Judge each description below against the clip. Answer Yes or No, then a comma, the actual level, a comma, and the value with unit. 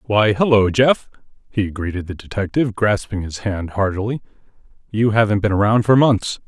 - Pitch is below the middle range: Yes, low, 105 Hz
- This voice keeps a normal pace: Yes, average, 160 wpm